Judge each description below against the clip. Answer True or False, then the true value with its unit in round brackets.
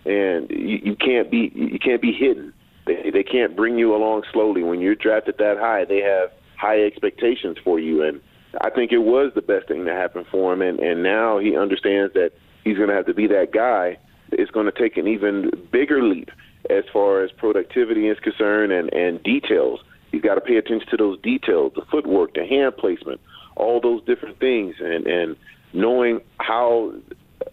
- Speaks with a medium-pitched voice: False (125 Hz)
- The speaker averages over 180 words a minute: True (200 wpm)